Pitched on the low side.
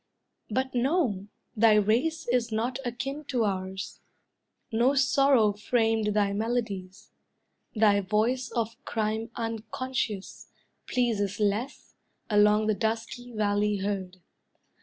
No: high, 220 Hz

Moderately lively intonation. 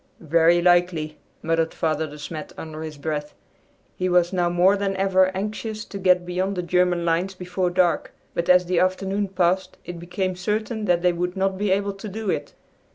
No: narrow, 2.0 semitones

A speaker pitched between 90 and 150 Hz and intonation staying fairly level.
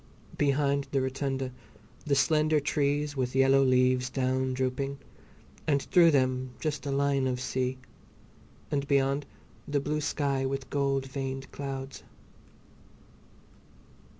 Yes: low, 135 Hz; narrow, 1.3 semitones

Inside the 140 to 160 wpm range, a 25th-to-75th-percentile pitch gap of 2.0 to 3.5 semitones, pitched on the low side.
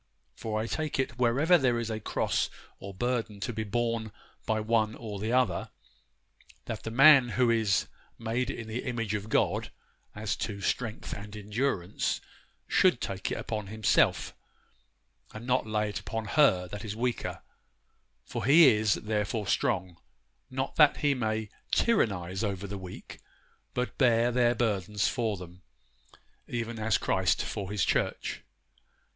Yes: average, 150 wpm; average, 2.7 semitones; low, 110 Hz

